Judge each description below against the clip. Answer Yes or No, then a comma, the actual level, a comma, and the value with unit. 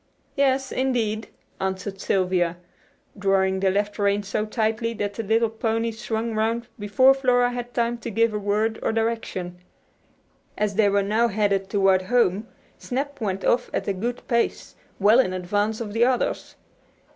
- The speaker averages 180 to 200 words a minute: No, average, 160 wpm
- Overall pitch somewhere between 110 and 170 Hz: No, high, 220 Hz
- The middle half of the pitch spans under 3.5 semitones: Yes, average, 2.9 semitones